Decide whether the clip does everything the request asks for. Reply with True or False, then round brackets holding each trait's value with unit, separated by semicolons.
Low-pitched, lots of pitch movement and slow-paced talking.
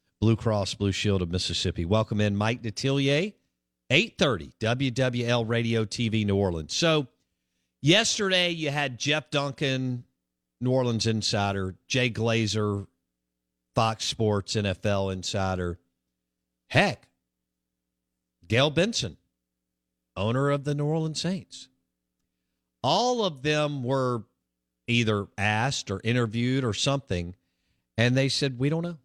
True (110 Hz; 7.3 semitones; 110 wpm)